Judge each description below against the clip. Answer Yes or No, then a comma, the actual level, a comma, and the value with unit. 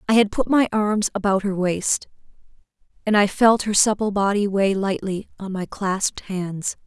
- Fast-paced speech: No, average, 175 wpm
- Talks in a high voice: Yes, high, 200 Hz